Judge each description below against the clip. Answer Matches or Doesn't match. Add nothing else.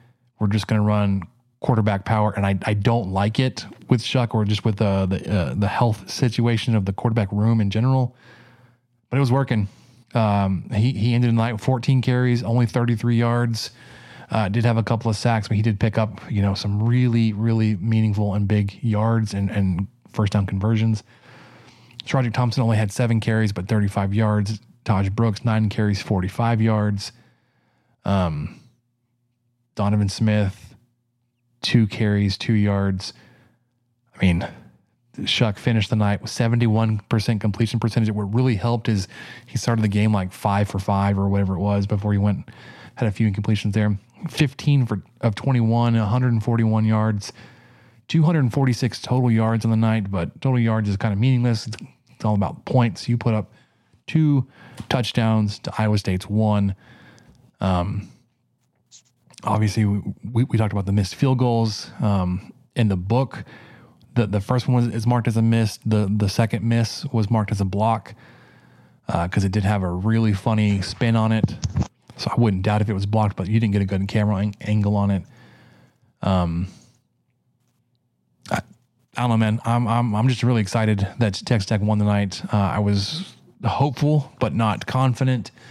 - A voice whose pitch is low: Matches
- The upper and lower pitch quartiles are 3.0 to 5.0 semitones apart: Doesn't match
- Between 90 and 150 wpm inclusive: Doesn't match